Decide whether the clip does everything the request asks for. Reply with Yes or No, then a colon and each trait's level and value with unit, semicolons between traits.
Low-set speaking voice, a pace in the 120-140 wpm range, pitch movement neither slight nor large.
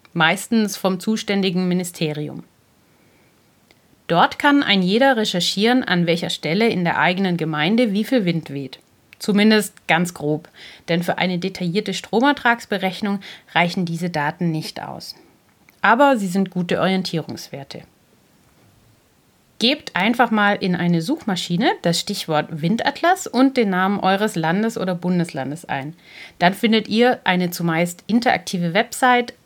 No: medium, 185 Hz; slow, 125 wpm; average, 4.3 semitones